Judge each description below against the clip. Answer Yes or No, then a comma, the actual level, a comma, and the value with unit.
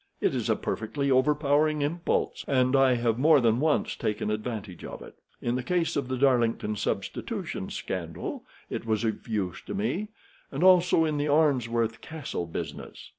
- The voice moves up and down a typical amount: Yes, average, 5.0 semitones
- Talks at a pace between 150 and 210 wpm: Yes, average, 170 wpm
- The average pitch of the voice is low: Yes, low, 130 Hz